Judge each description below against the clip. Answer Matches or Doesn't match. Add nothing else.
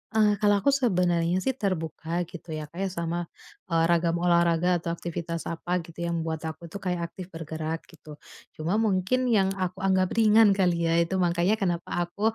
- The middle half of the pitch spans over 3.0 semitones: Doesn't match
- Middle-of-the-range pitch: Matches